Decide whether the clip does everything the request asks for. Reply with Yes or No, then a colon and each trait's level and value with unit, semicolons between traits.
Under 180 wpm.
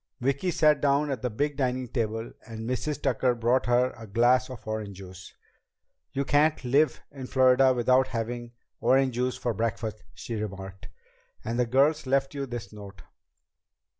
Yes: average, 165 wpm